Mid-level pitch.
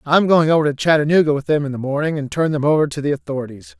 Yes: medium, 150 Hz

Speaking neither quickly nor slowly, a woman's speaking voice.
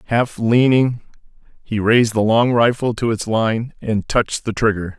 No: average, 170 wpm; male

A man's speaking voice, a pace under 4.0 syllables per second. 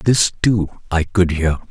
Yes: male; 3.5 syllables/s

